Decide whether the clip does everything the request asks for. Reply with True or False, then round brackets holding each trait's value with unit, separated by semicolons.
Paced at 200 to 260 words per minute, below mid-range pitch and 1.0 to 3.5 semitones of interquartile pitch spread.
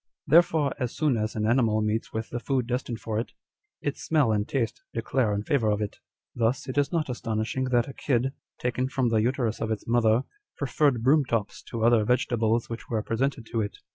True (205 wpm; 120 Hz; 2.9 semitones)